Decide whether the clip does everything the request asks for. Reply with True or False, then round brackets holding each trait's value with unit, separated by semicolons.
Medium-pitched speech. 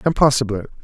False (125 Hz)